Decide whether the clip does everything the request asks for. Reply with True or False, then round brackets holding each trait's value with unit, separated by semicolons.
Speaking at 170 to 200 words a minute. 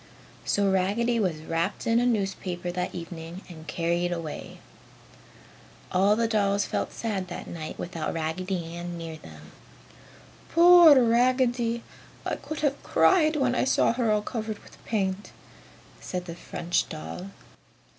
False (140 wpm)